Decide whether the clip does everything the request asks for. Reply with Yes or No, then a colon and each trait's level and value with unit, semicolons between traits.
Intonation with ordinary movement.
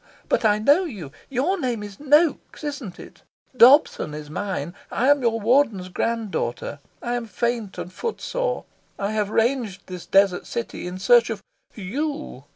No: wide, 6.2 semitones